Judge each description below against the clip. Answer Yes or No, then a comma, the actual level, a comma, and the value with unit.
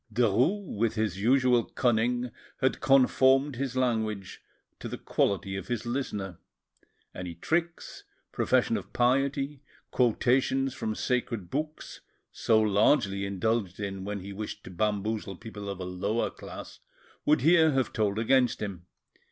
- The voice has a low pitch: Yes, low, 115 Hz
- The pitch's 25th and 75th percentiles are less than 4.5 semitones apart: No, average, 4.8 semitones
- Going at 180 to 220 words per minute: No, slow, 135 wpm